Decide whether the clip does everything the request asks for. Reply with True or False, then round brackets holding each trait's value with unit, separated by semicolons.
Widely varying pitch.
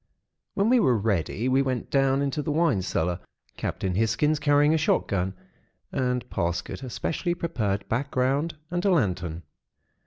True (7.0 semitones)